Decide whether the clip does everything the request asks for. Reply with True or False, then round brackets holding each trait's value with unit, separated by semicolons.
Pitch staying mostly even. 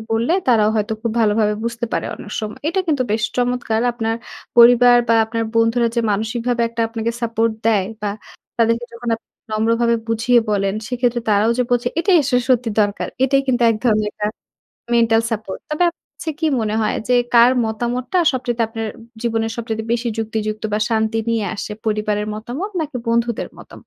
True (1.8 semitones)